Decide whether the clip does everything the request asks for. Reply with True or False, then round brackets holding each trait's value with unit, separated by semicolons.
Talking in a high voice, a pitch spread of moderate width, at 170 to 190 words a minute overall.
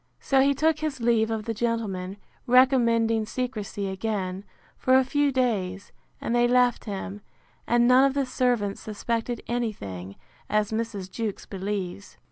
False (230 Hz; 3.8 semitones; 150 wpm)